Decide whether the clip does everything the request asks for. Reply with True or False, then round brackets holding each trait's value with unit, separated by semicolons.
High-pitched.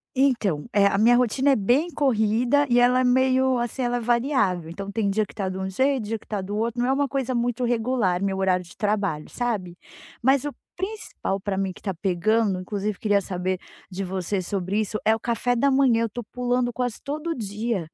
True (225 Hz)